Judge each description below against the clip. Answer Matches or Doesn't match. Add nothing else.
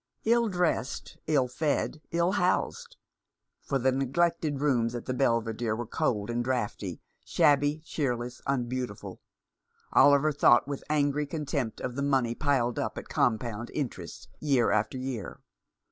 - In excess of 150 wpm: Doesn't match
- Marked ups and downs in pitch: Doesn't match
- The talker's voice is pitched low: Matches